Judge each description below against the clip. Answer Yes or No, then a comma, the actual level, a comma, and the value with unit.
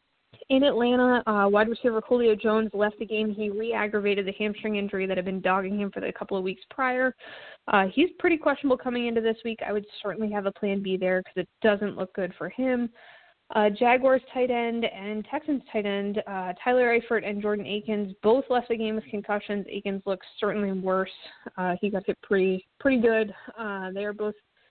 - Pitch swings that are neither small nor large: Yes, average, 3.0 semitones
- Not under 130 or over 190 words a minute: No, fast, 205 wpm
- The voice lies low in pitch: No, high, 210 Hz